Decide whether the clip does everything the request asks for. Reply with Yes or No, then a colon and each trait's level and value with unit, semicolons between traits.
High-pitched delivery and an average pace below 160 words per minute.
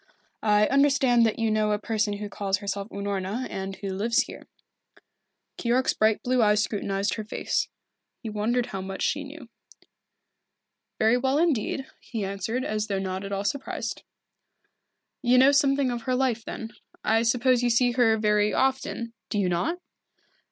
No: high, 225 Hz; average, 165 wpm